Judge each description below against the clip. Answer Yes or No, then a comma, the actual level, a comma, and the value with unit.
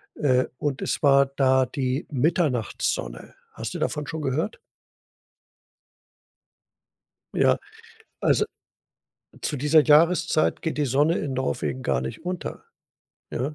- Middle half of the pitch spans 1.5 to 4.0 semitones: Yes, average, 3.2 semitones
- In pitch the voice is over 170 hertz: No, medium, 140 Hz